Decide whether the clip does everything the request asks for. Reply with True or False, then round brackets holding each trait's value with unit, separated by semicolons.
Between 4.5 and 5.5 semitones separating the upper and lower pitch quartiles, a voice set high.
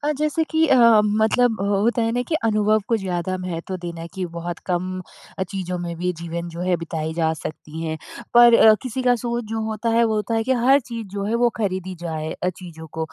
True (5.2 semitones; 195 Hz)